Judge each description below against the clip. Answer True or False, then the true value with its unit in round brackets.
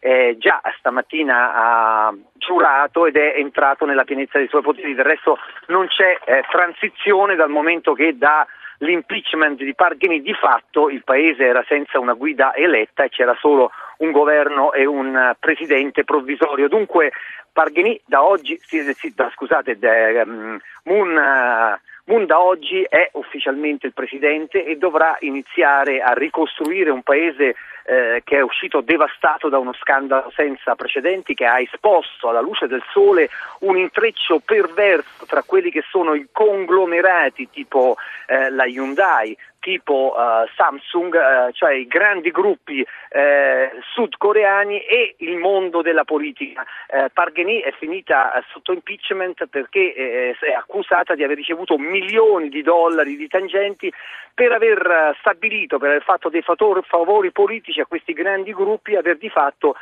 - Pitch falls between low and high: True (175 Hz)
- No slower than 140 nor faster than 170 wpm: True (150 wpm)